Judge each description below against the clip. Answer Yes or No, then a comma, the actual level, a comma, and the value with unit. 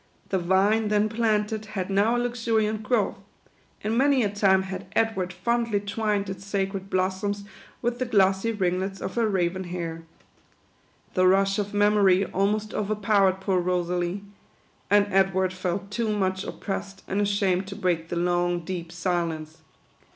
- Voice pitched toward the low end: No, high, 195 Hz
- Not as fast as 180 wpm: Yes, average, 150 wpm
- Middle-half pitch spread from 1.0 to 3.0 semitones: Yes, narrow, 2.4 semitones